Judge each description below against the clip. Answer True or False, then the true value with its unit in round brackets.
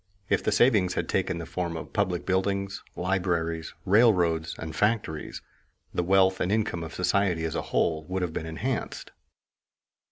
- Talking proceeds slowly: False (160 wpm)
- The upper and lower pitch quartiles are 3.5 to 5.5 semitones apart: False (2.9 semitones)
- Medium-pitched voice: False (90 Hz)